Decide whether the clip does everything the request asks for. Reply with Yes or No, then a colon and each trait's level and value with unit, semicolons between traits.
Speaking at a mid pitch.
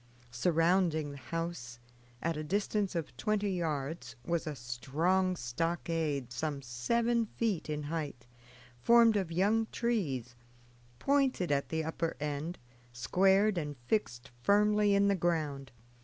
Yes: medium, 165 Hz